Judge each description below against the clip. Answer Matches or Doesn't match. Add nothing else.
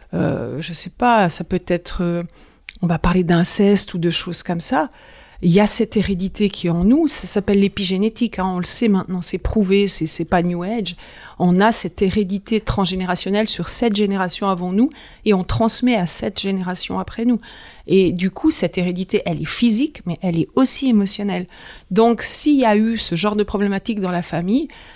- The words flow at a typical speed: Matches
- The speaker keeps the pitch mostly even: Doesn't match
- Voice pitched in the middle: Doesn't match